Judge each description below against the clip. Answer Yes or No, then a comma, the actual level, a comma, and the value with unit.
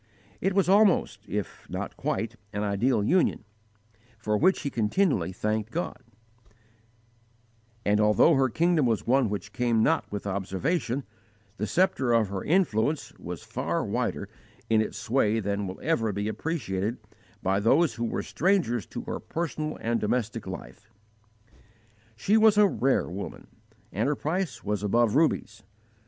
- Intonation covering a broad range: Yes, wide, 7.2 semitones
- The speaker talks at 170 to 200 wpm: No, average, 145 wpm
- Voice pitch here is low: Yes, low, 115 Hz